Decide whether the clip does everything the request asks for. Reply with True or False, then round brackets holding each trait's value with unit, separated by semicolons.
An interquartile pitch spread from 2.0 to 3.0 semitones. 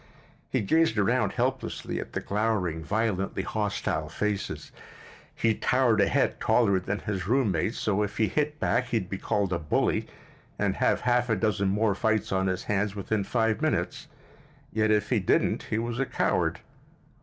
True (2.6 semitones)